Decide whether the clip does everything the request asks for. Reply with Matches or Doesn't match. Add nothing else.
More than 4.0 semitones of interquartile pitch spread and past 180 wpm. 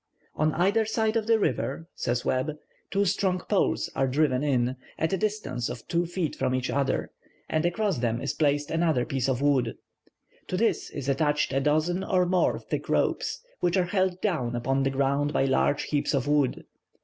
Matches